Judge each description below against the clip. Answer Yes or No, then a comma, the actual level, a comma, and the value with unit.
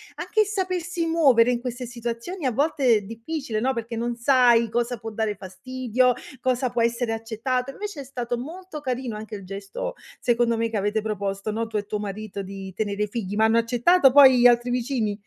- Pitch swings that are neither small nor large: Yes, average, 3.1 semitones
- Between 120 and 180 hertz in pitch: No, high, 235 Hz